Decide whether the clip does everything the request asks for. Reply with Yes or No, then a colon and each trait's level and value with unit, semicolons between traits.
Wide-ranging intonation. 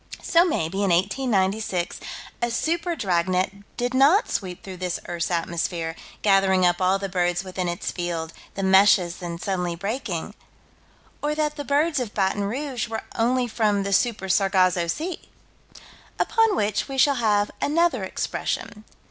Yes: wide, 5.7 semitones